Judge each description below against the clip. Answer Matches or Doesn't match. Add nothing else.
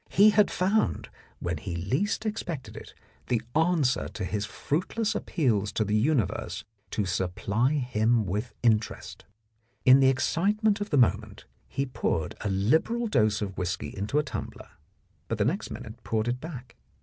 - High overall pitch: Doesn't match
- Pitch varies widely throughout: Matches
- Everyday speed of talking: Matches